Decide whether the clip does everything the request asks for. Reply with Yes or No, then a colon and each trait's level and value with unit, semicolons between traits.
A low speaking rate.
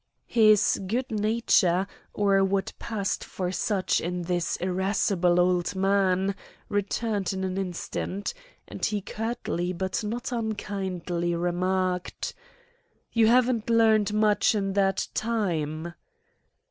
Yes: slow, 110 wpm